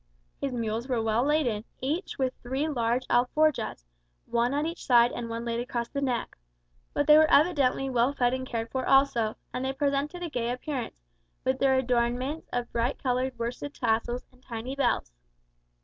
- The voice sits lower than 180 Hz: No, very high, 255 Hz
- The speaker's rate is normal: Yes, average, 180 wpm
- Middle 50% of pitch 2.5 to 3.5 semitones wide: Yes, average, 2.8 semitones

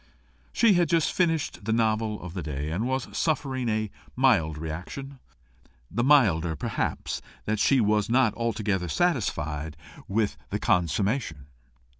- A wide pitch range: Yes, wide, 7.2 semitones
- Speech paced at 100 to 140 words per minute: Yes, slow, 135 wpm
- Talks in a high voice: No, low, 110 Hz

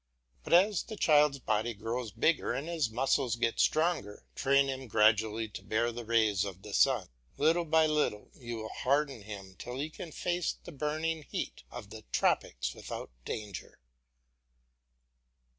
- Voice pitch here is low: Yes, low, 125 Hz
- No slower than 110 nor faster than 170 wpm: Yes, average, 160 wpm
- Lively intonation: Yes, wide, 5.9 semitones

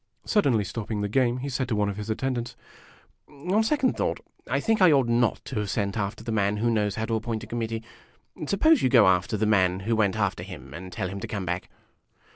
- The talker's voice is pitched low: Yes, low, 110 Hz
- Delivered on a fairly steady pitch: No, average, 3.9 semitones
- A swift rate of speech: Yes, fast, 235 wpm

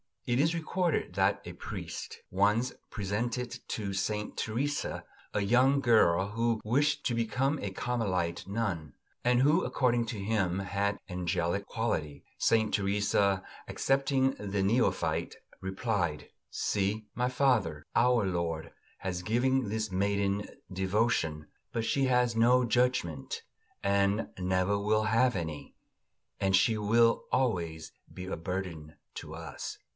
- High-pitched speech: No, low, 105 Hz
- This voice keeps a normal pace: No, slow, 130 wpm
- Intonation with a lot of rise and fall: No, average, 4.5 semitones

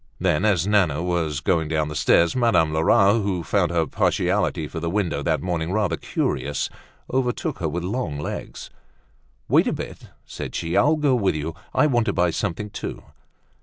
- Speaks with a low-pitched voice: Yes, very low, 90 Hz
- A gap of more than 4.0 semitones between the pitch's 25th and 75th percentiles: Yes, average, 4.5 semitones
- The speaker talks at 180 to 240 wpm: Yes, average, 185 wpm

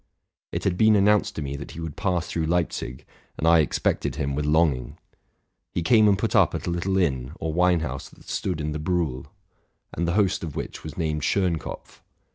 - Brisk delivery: Yes, fast, 220 wpm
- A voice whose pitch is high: No, very low, 80 Hz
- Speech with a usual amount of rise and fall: Yes, average, 3.3 semitones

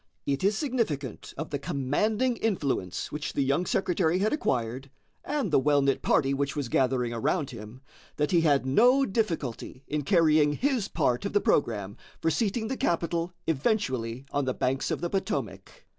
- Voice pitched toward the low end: No, medium, 150 Hz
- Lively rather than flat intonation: Yes, wide, 6.8 semitones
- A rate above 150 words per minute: Yes, average, 175 wpm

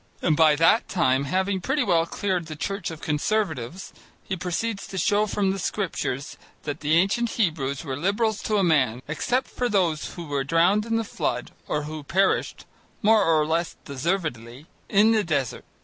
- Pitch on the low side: No, medium, 170 Hz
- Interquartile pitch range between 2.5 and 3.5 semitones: No, average, 5.2 semitones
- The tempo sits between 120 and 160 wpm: No, average, 175 wpm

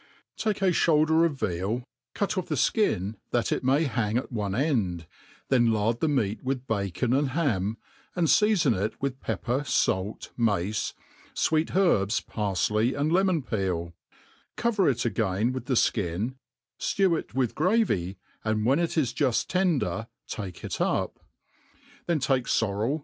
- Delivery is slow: No, average, 155 wpm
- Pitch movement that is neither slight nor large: No, wide, 6.8 semitones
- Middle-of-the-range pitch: No, low, 125 Hz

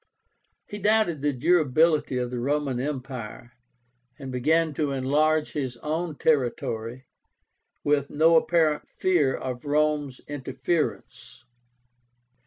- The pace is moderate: No, slow, 105 wpm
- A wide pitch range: No, average, 3.3 semitones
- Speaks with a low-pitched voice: No, medium, 145 Hz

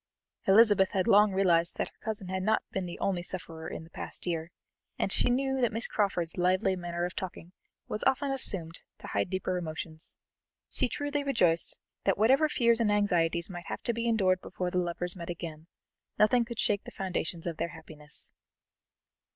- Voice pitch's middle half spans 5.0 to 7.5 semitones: No, average, 4.3 semitones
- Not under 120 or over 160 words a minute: No, average, 185 wpm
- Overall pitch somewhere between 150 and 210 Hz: Yes, medium, 185 Hz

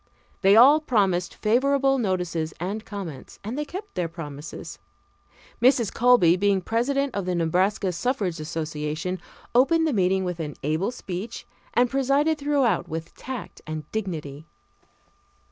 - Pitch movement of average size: No, wide, 6.9 semitones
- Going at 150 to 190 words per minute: No, slow, 135 wpm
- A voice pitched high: Yes, high, 195 Hz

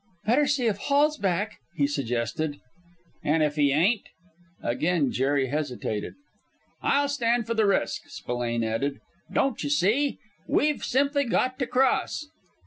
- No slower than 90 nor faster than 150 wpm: Yes, average, 140 wpm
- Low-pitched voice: No, high, 190 Hz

